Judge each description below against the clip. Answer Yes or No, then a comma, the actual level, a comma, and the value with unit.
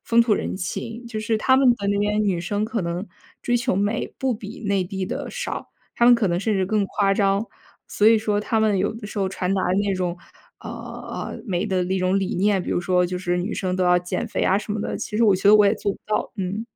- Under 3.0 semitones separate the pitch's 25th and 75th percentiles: Yes, narrow, 2.6 semitones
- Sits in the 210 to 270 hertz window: No, high, 200 Hz